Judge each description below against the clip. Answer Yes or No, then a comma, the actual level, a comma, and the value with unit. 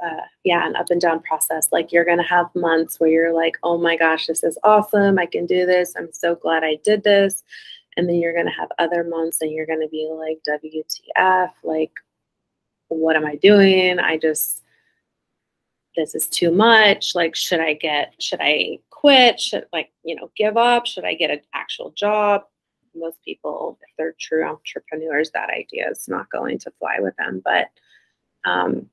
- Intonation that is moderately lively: Yes, average, 3.6 semitones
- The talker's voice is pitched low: No, medium, 170 Hz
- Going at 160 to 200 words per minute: Yes, average, 190 wpm